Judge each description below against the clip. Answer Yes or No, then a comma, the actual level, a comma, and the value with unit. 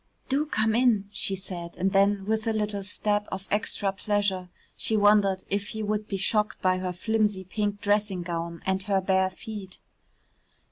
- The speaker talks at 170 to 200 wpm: Yes, average, 175 wpm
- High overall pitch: Yes, high, 200 Hz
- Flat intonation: Yes, narrow, 2.0 semitones